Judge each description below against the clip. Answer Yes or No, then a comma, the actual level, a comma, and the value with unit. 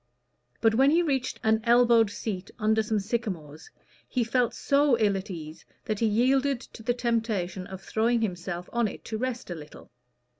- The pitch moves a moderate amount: Yes, average, 3.8 semitones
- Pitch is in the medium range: No, high, 225 Hz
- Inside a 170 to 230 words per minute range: Yes, average, 180 wpm